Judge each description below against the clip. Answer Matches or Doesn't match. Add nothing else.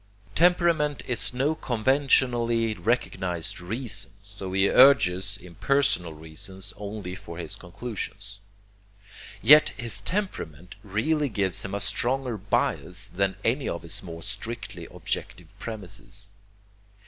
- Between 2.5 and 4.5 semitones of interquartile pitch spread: Doesn't match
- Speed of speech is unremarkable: Doesn't match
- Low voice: Matches